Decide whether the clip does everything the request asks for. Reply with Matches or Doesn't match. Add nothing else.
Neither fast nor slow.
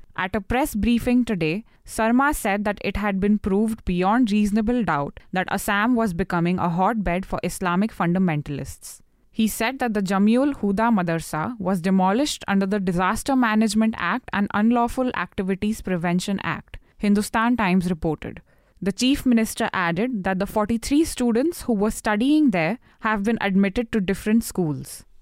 Matches